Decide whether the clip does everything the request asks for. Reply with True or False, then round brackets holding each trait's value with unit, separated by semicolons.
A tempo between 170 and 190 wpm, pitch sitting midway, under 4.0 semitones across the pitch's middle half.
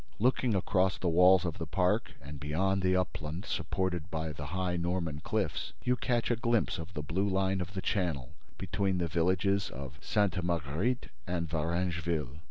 False (175 wpm; 90 Hz; 3.0 semitones)